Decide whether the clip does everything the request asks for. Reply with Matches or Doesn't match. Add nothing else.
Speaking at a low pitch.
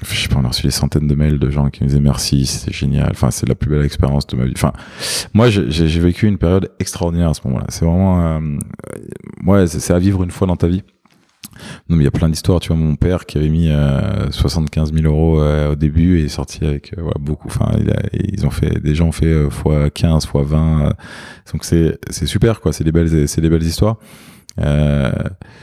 Matches